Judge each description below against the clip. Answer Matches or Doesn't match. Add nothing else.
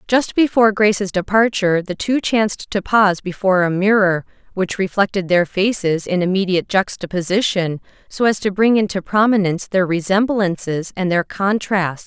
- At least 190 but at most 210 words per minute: Doesn't match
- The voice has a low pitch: Doesn't match